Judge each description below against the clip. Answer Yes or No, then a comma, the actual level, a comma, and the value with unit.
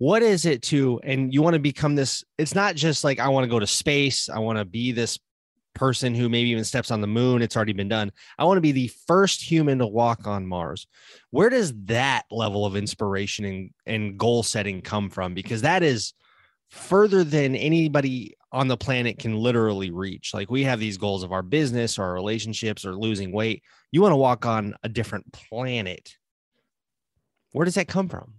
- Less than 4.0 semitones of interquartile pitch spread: No, average, 4.9 semitones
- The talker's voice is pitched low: Yes, low, 120 Hz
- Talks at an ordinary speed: No, fast, 210 wpm